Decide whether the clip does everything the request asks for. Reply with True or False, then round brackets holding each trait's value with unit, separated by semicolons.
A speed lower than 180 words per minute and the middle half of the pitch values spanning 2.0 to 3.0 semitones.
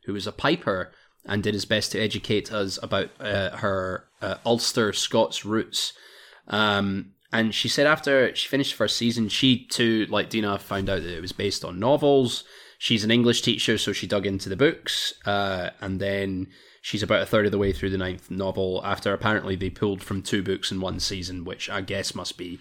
False (205 wpm; 2.7 semitones)